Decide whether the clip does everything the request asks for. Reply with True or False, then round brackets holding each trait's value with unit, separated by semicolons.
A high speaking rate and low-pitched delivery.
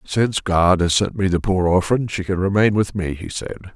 True (240 wpm; 95 Hz)